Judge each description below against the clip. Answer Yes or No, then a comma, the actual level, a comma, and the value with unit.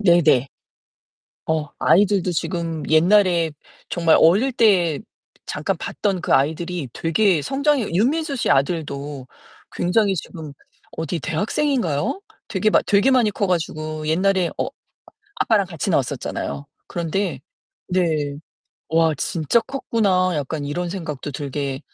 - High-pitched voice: No, medium, 175 Hz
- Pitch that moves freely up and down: No, average, 4.6 semitones